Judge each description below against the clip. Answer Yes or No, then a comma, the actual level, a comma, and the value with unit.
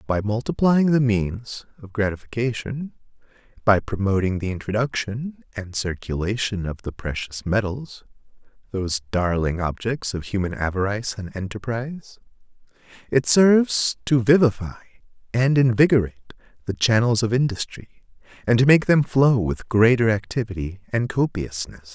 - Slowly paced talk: Yes, slow, 120 wpm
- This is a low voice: Yes, low, 110 Hz